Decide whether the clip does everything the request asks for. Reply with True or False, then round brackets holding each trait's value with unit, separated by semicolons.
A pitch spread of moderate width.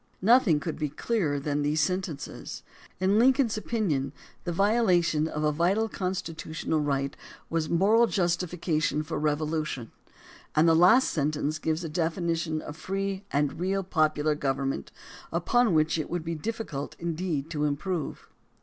True (3.7 semitones)